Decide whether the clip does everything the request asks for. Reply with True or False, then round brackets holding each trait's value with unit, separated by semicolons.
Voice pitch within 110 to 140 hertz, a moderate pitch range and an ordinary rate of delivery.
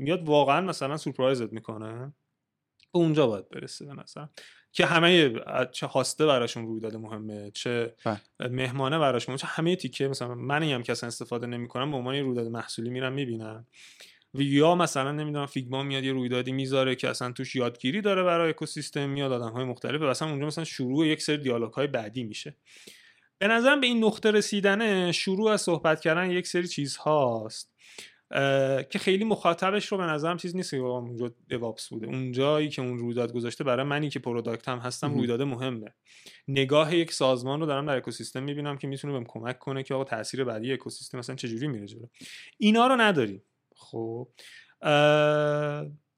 False (135 Hz; 4.1 semitones; 170 wpm)